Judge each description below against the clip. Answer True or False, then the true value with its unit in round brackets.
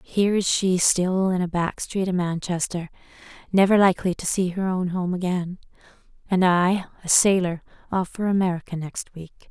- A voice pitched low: False (180 Hz)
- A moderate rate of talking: True (170 wpm)